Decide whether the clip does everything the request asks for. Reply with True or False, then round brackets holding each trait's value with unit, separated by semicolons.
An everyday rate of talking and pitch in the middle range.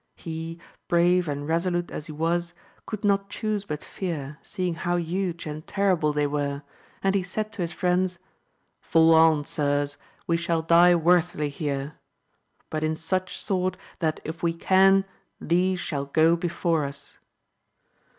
True (150 wpm; 170 Hz)